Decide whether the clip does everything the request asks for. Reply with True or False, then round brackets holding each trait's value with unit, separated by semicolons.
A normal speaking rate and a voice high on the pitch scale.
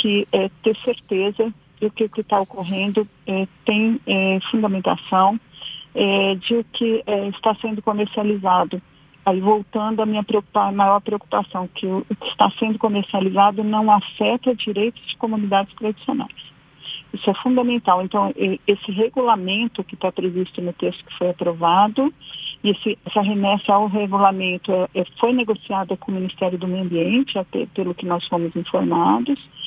True (155 wpm; 200 Hz)